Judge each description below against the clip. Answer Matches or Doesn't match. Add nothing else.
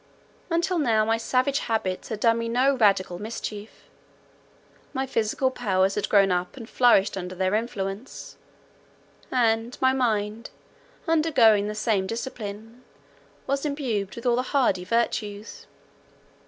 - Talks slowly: Matches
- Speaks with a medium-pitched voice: Doesn't match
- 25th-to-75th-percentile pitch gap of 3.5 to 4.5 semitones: Matches